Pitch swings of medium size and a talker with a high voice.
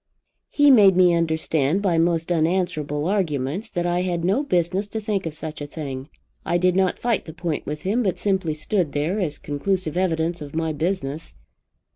No: average, 3.5 semitones; medium, 175 Hz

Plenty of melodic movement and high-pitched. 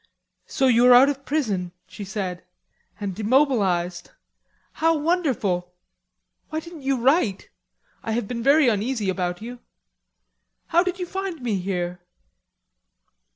Yes: wide, 7.1 semitones; high, 240 Hz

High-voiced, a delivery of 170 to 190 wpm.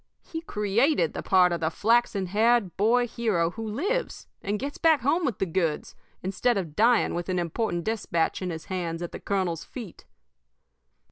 Yes: high, 200 Hz; average, 180 wpm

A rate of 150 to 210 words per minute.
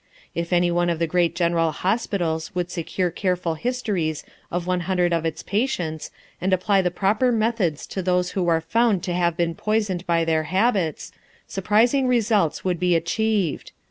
Yes: average, 175 wpm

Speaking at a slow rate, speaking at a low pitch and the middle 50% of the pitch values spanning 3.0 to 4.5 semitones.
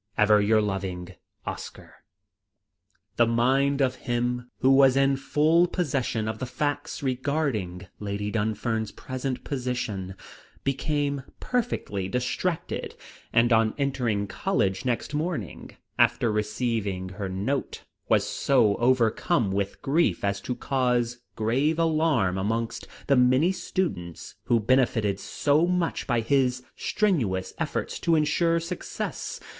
No: slow, 120 wpm; low, 125 Hz; average, 5.0 semitones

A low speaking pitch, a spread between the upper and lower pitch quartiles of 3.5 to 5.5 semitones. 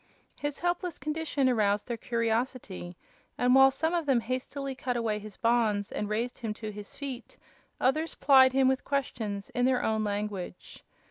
No: high, 245 Hz; average, 4.1 semitones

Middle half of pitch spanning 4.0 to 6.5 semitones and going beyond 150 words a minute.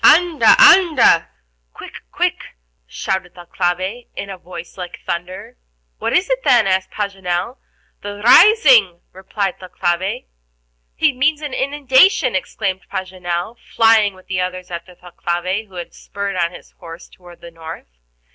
No: average, 5.0 semitones; slow, 135 wpm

